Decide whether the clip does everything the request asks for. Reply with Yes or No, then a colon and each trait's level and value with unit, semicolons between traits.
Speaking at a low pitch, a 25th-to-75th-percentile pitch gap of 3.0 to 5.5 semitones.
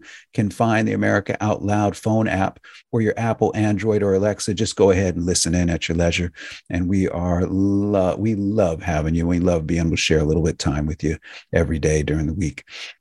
Yes: very low, 95 Hz; average, 3.7 semitones